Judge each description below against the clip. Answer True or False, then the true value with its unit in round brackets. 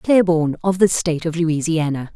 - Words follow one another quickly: False (165 wpm)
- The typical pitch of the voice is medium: True (165 Hz)